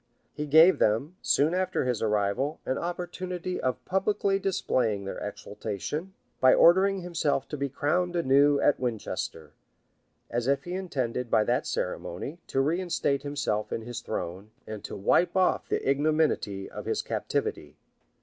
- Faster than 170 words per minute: No, average, 150 wpm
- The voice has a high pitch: No, medium, 140 Hz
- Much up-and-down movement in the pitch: Yes, wide, 7.2 semitones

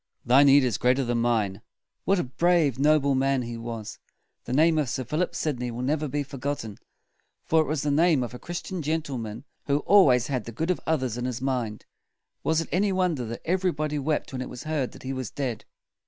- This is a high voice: No, low, 135 Hz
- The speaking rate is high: Yes, fast, 230 wpm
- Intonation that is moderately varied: Yes, average, 4.2 semitones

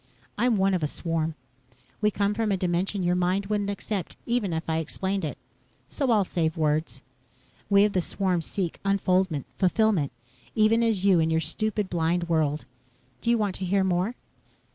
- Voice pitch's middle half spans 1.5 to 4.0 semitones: Yes, average, 3.6 semitones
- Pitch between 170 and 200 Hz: Yes, high, 190 Hz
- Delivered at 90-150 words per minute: No, average, 180 wpm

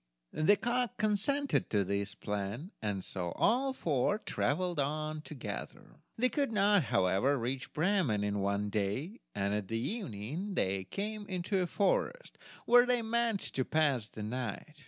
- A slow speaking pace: No, average, 150 wpm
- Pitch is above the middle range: No, medium, 155 Hz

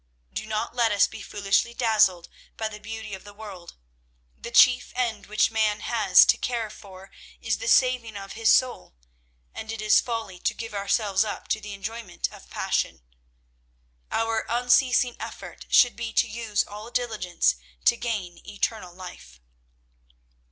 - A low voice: No, high, 215 Hz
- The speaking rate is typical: Yes, average, 160 wpm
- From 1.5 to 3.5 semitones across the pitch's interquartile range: Yes, average, 2.7 semitones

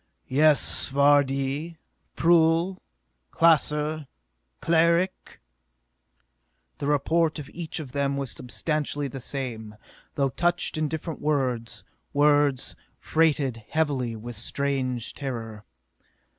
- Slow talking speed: Yes, slow, 95 wpm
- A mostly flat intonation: No, average, 3.3 semitones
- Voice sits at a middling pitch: Yes, medium, 145 Hz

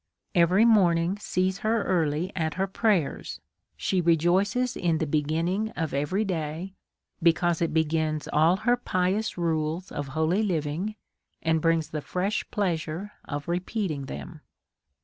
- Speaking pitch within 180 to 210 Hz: No, medium, 170 Hz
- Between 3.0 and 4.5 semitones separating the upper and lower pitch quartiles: Yes, average, 3.5 semitones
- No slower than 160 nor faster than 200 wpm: No, average, 140 wpm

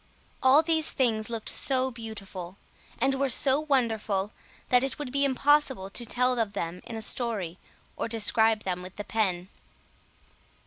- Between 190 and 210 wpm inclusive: No, average, 155 wpm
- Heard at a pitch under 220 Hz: No, high, 230 Hz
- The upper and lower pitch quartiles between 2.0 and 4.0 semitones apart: No, average, 4.7 semitones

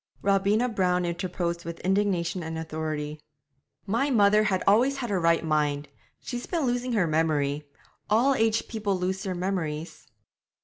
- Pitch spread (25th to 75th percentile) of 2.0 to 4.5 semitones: No, average, 4.9 semitones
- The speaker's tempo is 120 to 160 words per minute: Yes, average, 145 wpm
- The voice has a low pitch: No, medium, 185 Hz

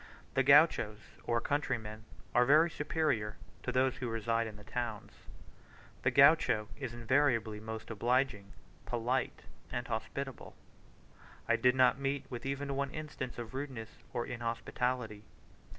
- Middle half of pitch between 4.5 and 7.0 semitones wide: No, average, 3.5 semitones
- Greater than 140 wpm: No, slow, 135 wpm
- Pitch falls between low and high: No, low, 125 Hz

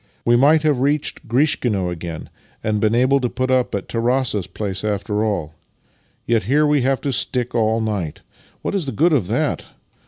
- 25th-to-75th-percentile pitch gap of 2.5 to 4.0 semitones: No, average, 4.6 semitones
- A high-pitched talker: No, low, 120 Hz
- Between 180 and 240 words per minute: Yes, average, 185 wpm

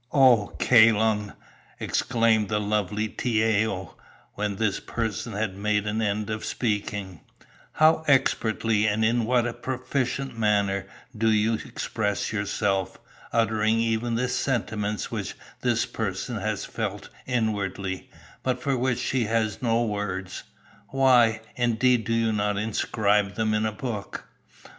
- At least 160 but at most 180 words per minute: No, slow, 135 wpm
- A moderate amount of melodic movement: No, narrow, 2.2 semitones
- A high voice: No, low, 110 Hz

